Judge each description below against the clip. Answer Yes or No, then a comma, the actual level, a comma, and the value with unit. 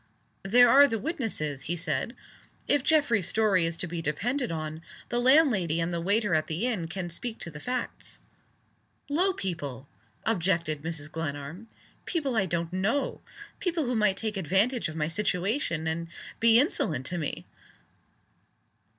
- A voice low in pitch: No, medium, 185 Hz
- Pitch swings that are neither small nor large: No, wide, 6.8 semitones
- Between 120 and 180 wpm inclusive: Yes, average, 155 wpm